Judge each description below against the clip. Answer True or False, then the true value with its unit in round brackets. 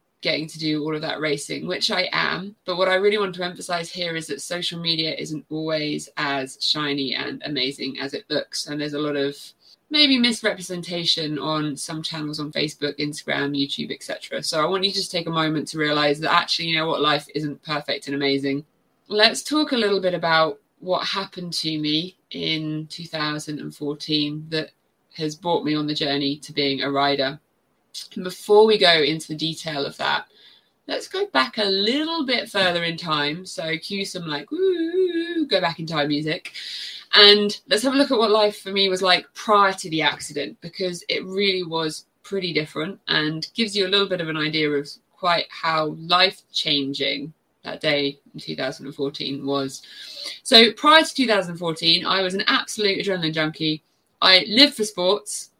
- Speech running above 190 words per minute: False (185 wpm)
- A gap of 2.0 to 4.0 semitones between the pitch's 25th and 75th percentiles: False (4.6 semitones)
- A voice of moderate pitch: True (160 Hz)